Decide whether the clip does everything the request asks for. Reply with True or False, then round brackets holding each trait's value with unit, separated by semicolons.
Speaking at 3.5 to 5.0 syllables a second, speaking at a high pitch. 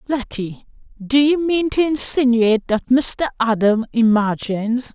True (4.3 syllables/s; 245 Hz)